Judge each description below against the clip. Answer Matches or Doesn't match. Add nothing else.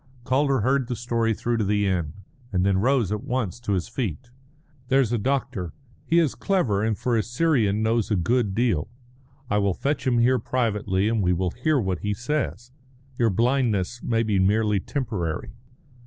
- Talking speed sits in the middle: Matches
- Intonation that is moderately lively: Matches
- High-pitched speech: Doesn't match